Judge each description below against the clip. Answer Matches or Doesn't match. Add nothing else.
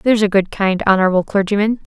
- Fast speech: Doesn't match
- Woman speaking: Matches